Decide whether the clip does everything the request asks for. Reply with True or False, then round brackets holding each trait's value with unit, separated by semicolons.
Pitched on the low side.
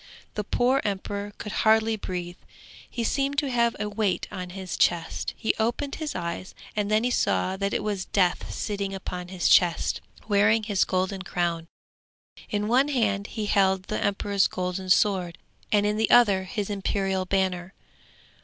False (200 Hz)